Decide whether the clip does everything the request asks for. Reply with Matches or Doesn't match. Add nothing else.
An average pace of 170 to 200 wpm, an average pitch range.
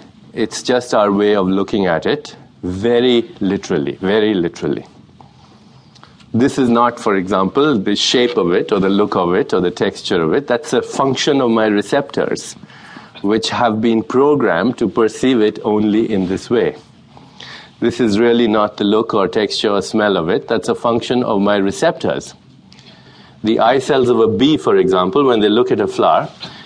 Matches